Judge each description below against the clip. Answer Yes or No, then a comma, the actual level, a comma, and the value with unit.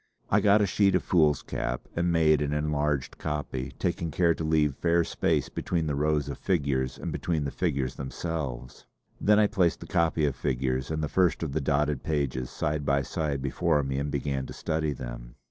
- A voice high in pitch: No, very low, 75 Hz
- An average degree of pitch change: Yes, average, 3.2 semitones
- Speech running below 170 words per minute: No, average, 195 wpm